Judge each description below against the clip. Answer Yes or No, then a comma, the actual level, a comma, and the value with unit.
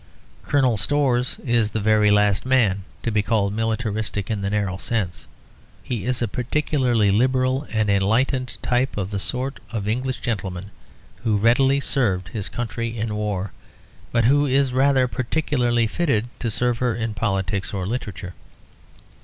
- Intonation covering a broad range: No, average, 3.7 semitones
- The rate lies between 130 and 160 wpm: Yes, average, 155 wpm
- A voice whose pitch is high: No, low, 115 Hz